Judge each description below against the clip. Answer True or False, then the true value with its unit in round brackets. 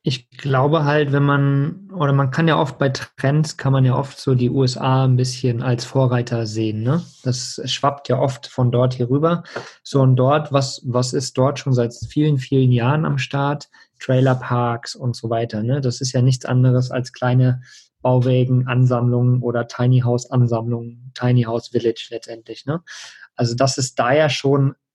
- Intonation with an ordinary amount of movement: False (2.2 semitones)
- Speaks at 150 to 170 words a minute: False (185 wpm)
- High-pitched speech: False (130 Hz)